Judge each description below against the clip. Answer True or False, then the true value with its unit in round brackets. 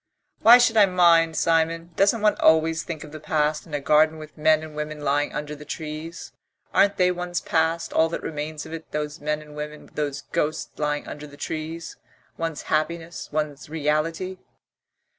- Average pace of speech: True (180 wpm)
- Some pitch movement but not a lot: False (1.7 semitones)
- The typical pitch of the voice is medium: True (155 Hz)